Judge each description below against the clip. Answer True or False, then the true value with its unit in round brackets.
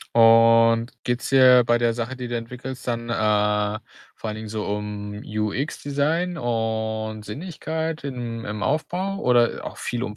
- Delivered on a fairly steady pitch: False (3.2 semitones)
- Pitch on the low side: True (115 Hz)